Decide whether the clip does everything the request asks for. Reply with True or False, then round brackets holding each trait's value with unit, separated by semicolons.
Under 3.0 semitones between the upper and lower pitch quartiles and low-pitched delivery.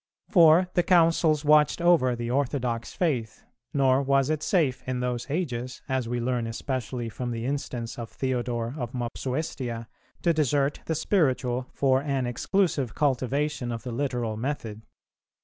False (3.6 semitones; 130 Hz)